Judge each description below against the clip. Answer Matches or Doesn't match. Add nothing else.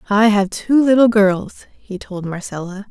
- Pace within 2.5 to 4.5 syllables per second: Matches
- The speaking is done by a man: Doesn't match